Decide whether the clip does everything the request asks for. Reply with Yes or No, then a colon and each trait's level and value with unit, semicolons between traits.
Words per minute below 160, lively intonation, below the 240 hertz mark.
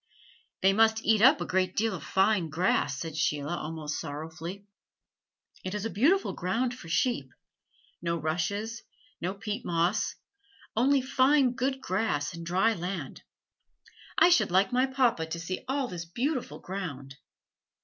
Yes: average, 150 wpm; wide, 6.2 semitones; high, 190 Hz